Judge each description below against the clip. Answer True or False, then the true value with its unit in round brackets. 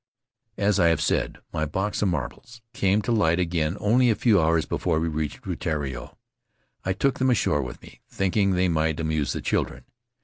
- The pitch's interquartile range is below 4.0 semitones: False (4.8 semitones)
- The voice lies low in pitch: True (90 Hz)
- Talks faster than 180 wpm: True (190 wpm)